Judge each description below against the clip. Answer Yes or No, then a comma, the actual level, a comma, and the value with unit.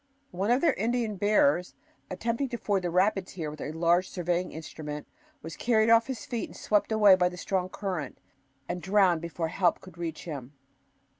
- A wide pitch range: No, average, 4.0 semitones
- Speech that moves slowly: No, average, 180 wpm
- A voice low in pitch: No, medium, 185 Hz